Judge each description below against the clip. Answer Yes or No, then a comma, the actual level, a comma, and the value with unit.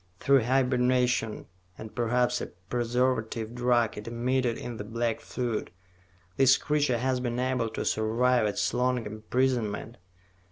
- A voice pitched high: No, low, 120 Hz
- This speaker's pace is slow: Yes, slow, 130 wpm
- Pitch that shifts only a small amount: Yes, narrow, 2.1 semitones